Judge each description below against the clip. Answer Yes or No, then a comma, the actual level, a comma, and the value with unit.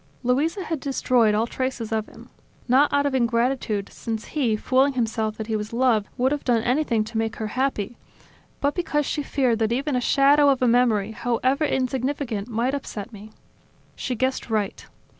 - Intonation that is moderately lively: Yes, average, 3.6 semitones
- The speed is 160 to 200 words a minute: Yes, average, 180 wpm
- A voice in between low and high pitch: No, high, 245 Hz